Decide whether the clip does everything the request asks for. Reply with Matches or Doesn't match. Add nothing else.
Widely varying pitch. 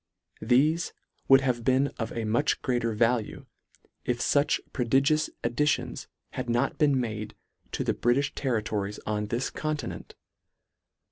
Doesn't match